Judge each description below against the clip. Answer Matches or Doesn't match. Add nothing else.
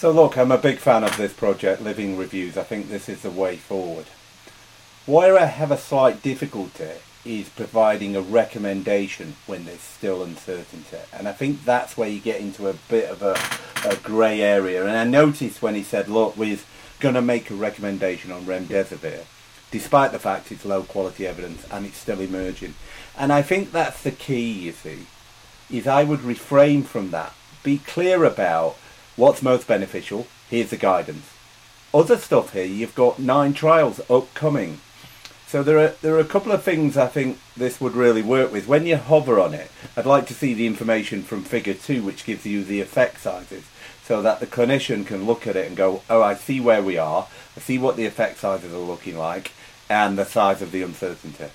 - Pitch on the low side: Matches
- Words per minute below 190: Doesn't match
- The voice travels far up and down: Matches